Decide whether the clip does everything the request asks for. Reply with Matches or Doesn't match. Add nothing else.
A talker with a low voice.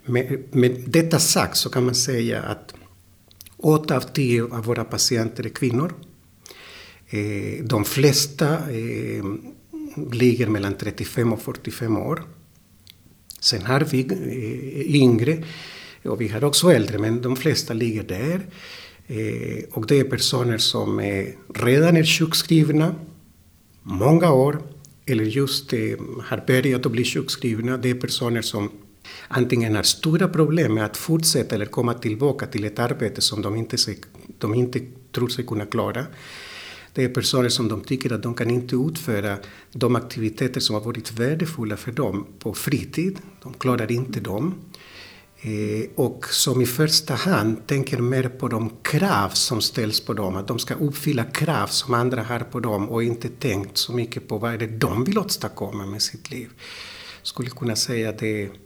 Matches